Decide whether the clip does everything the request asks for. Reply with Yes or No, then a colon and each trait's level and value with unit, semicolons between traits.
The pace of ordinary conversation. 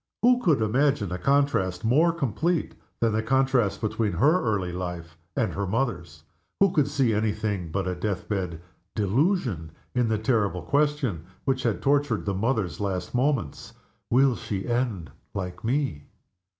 Yes: average, 155 wpm